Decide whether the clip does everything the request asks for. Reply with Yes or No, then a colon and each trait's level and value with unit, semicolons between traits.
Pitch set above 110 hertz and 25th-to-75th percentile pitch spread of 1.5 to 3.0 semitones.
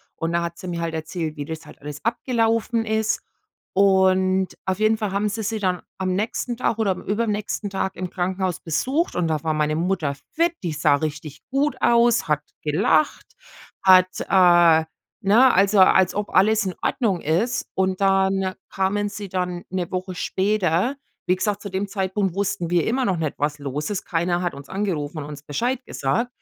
No: high, 190 Hz; average, 3.8 semitones